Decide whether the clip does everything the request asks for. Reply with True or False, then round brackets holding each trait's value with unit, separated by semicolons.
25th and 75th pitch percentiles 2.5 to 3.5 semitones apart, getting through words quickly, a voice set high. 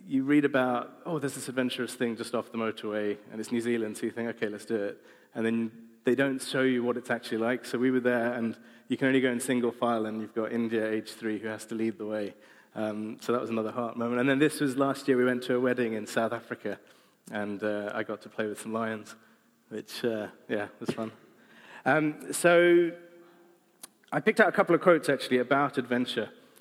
False (3.1 semitones; 235 wpm; 120 Hz)